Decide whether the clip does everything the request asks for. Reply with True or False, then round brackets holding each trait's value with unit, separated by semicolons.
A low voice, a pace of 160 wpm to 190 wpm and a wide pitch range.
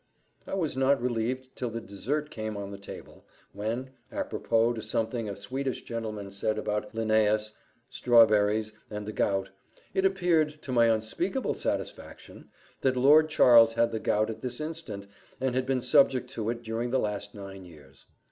False (115 Hz; 165 wpm; 3.5 semitones)